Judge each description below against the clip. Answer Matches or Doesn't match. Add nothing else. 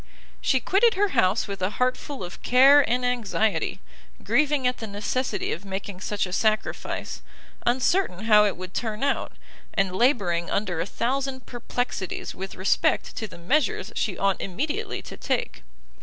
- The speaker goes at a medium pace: Matches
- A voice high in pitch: Matches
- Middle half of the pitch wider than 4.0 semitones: Matches